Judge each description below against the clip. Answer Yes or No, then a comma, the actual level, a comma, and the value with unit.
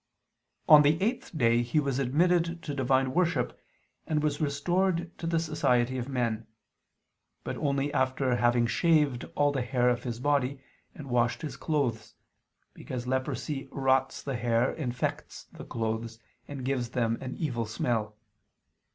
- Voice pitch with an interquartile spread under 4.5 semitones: Yes, average, 3.7 semitones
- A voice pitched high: No, low, 130 Hz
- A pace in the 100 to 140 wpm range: No, average, 150 wpm